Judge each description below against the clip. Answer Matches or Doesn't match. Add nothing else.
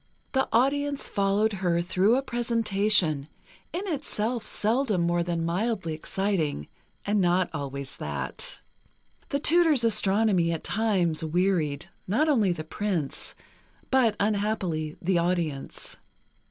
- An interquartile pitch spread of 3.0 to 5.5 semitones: Matches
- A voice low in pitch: Doesn't match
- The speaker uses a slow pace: Matches